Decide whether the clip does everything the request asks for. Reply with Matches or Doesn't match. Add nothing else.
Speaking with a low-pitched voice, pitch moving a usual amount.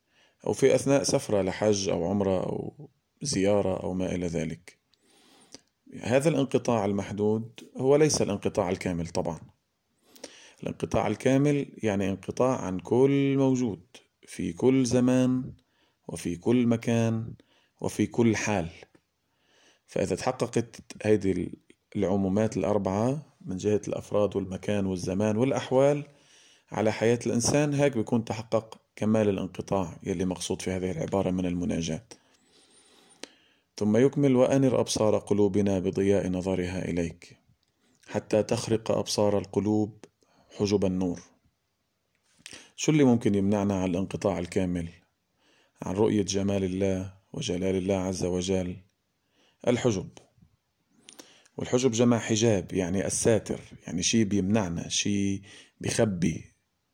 Matches